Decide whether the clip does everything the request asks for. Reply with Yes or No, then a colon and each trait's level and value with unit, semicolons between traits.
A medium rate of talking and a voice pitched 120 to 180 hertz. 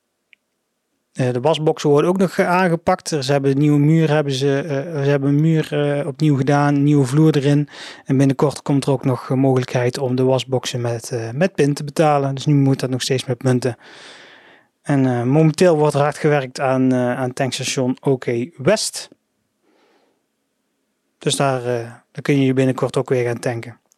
Yes: average, 185 wpm; medium, 140 Hz